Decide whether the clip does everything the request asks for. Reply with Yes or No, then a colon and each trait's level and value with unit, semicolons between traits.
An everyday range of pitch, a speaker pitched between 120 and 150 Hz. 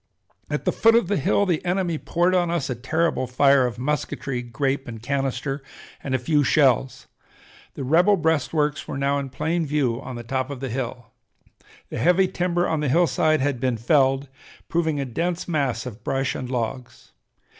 Yes: average, 4.2 semitones; medium, 140 Hz